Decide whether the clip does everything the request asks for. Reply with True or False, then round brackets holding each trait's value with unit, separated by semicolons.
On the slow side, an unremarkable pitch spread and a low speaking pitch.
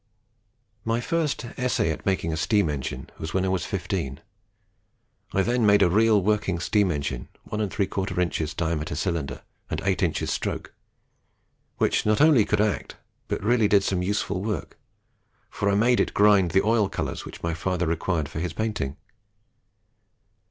False (160 wpm; 4.2 semitones; 95 Hz)